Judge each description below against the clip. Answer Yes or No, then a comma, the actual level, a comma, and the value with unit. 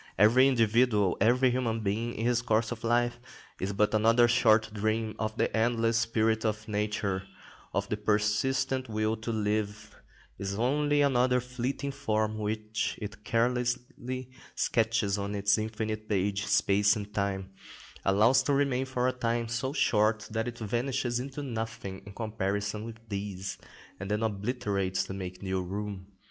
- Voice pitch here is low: Yes, low, 110 Hz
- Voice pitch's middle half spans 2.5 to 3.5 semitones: Yes, average, 2.8 semitones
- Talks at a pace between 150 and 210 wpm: Yes, average, 155 wpm